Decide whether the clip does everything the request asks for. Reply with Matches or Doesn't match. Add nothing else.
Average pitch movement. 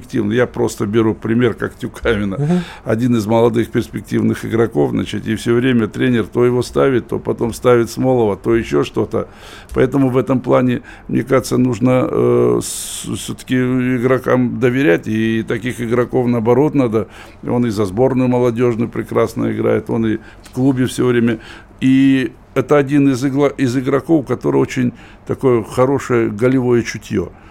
Doesn't match